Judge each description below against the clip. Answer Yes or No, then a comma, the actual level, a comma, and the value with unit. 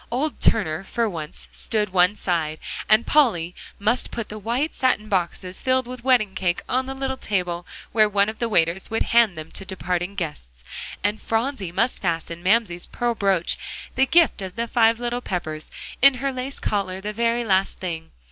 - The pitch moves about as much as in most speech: Yes, average, 5.0 semitones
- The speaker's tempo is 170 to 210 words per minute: Yes, average, 185 wpm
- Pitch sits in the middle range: No, high, 210 Hz